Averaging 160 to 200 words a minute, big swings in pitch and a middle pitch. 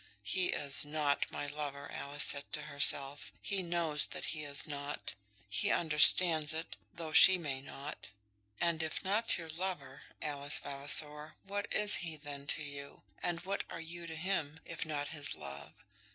No: average, 165 wpm; average, 2.9 semitones; medium, 150 Hz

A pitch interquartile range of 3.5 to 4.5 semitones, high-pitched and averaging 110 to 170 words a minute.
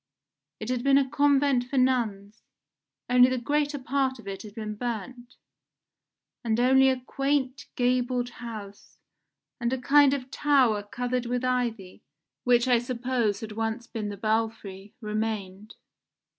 No: average, 3.0 semitones; high, 245 Hz; average, 145 wpm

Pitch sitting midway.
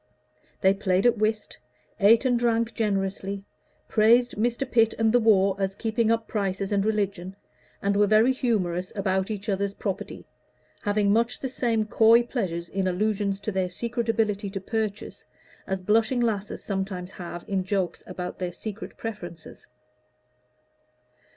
No: high, 205 Hz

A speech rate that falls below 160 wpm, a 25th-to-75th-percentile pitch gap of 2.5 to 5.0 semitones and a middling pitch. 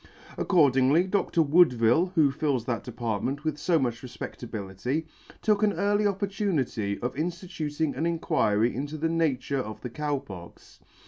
No: average, 140 wpm; wide, 5.4 semitones; medium, 145 Hz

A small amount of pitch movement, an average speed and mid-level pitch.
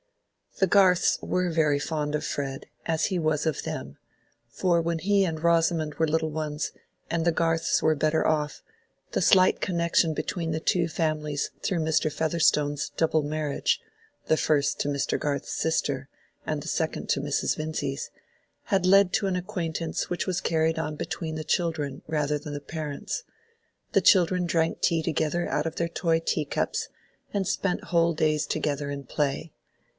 Yes: narrow, 2.1 semitones; average, 165 wpm; medium, 160 Hz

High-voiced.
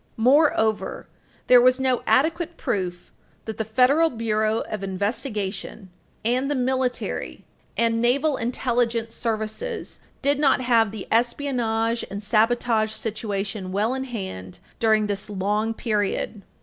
Yes: high, 225 Hz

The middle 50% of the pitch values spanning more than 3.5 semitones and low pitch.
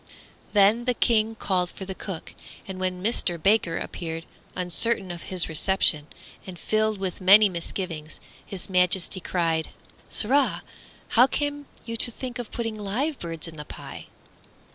No: average, 4.3 semitones; high, 190 Hz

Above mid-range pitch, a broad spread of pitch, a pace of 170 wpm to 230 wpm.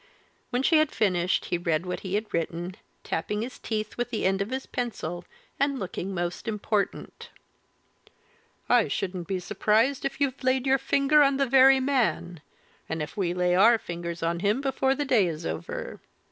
Yes: high, 210 Hz; wide, 6.9 semitones; average, 180 wpm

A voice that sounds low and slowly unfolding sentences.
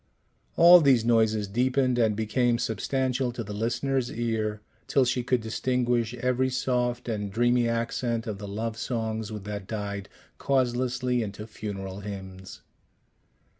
Yes: low, 115 Hz; slow, 130 wpm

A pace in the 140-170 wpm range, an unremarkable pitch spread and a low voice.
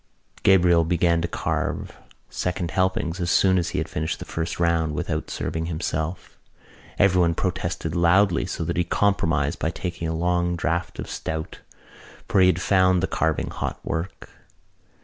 No: average, 160 wpm; narrow, 2.0 semitones; very low, 85 Hz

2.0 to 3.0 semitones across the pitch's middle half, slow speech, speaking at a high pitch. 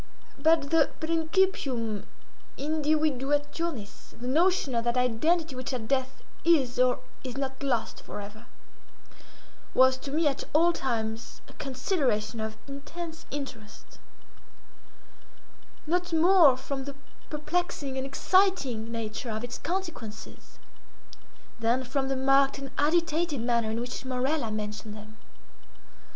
No: average, 5.0 semitones; slow, 115 wpm; very high, 270 Hz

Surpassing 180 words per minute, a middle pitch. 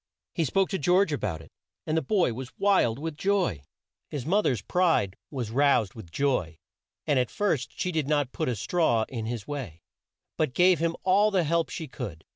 Yes: average, 195 wpm; medium, 145 Hz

